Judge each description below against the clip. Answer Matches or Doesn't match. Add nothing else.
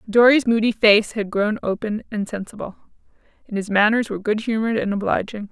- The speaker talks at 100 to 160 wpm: Doesn't match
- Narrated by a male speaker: Doesn't match